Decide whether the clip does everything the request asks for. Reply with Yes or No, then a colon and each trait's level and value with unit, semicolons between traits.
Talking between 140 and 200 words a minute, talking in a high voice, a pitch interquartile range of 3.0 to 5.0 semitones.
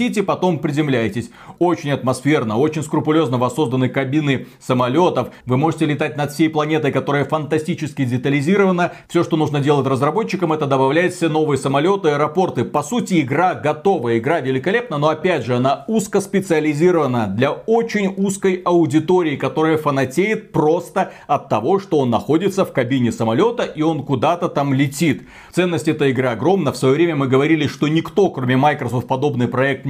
No: average, 155 wpm; medium, 155 Hz; average, 4.2 semitones